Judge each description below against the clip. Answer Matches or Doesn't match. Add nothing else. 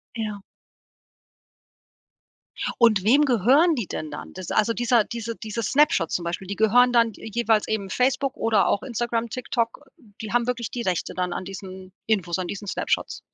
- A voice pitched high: Matches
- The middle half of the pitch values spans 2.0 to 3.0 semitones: Doesn't match